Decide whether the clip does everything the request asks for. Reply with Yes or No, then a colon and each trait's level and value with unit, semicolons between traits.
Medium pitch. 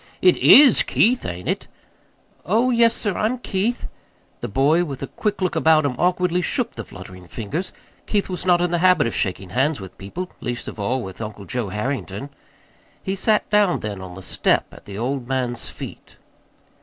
Yes: medium, 145 Hz